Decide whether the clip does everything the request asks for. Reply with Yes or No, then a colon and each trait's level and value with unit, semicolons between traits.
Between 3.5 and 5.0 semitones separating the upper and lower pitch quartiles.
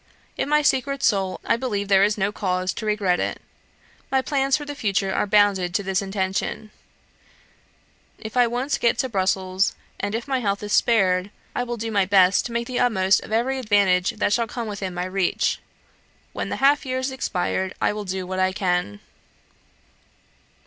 Yes: average, 4.2 semitones